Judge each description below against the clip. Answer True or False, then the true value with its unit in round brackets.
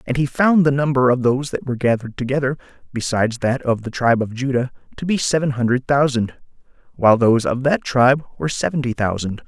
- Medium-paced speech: True (195 wpm)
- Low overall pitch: True (130 Hz)